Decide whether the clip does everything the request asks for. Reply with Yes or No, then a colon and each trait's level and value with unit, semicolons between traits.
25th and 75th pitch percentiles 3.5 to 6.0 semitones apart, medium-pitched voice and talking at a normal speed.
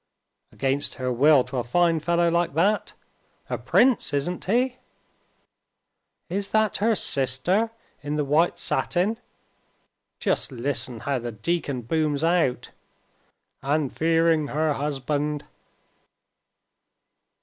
No: average, 4.2 semitones; medium, 150 Hz; slow, 110 wpm